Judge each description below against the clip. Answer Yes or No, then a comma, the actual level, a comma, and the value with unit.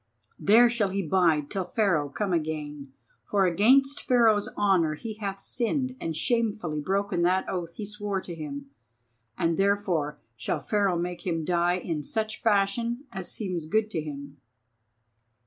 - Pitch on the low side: No, high, 190 Hz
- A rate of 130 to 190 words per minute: Yes, average, 150 wpm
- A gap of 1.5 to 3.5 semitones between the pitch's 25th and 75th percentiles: No, average, 4.6 semitones